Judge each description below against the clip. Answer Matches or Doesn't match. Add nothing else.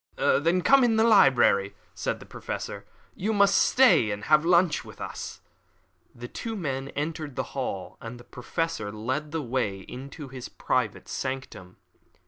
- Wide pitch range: Matches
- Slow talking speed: Doesn't match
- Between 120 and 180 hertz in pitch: Matches